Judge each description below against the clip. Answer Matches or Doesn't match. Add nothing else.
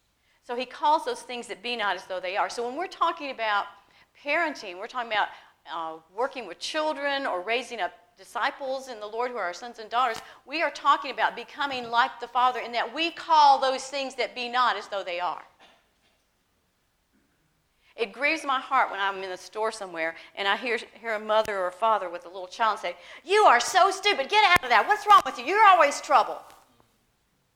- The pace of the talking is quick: Matches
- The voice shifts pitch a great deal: Matches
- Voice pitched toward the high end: Matches